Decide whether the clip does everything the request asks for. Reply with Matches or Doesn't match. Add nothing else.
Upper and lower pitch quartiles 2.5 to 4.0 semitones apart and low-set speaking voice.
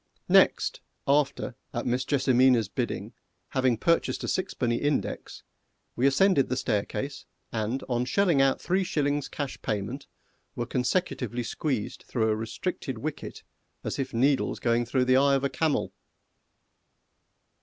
Matches